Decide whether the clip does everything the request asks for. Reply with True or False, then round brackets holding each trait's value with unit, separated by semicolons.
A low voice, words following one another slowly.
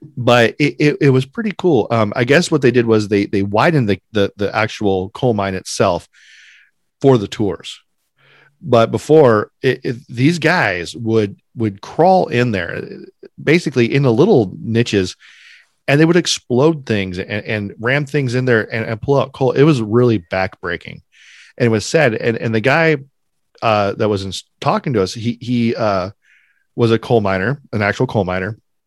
False (120 Hz; 185 wpm)